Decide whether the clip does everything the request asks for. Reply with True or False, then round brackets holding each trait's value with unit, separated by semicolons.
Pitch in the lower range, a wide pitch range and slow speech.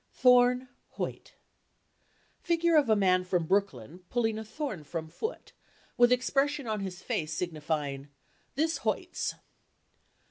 False (215 Hz; 7.5 semitones; 115 wpm)